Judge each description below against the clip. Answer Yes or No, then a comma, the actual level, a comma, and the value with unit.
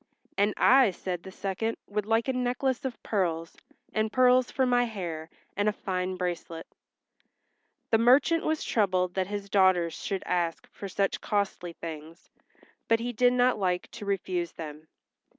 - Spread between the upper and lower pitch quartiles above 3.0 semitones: Yes, average, 5.1 semitones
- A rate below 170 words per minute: Yes, average, 160 wpm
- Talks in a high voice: Yes, high, 200 Hz